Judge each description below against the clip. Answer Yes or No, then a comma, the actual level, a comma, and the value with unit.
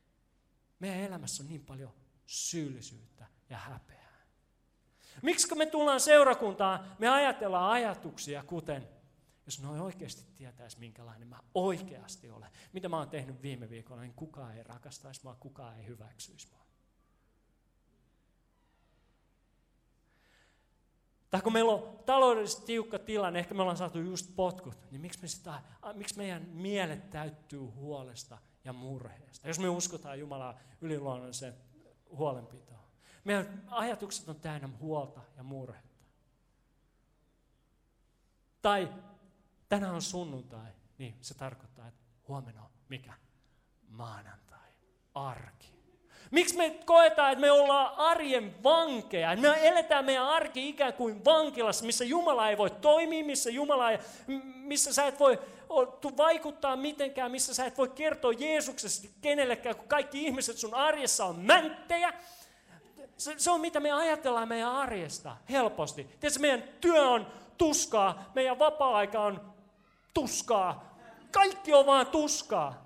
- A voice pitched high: Yes, high, 195 Hz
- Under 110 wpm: No, average, 125 wpm